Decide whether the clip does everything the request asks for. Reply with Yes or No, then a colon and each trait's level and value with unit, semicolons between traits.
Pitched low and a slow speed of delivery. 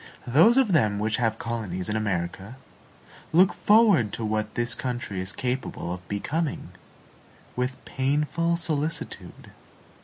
Yes: low, 120 Hz; slow, 125 wpm